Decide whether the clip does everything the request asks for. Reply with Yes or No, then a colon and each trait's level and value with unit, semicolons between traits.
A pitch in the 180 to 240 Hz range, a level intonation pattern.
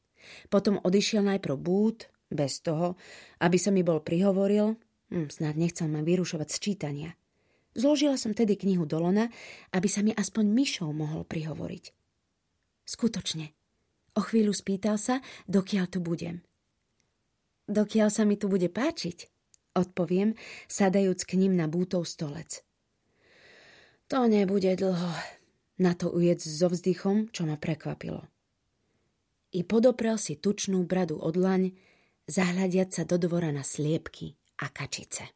No: medium, 185 Hz; average, 3.6 semitones